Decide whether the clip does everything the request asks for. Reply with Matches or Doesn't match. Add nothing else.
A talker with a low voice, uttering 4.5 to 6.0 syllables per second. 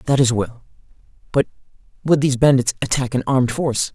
Doesn't match